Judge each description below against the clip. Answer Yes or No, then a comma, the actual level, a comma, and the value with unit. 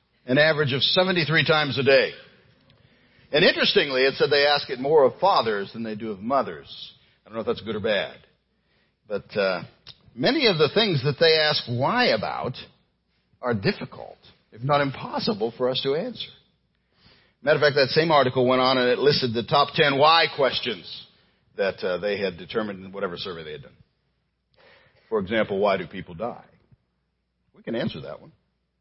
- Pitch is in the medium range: Yes, medium, 145 Hz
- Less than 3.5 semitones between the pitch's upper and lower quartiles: No, average, 4.0 semitones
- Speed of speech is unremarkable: Yes, average, 185 wpm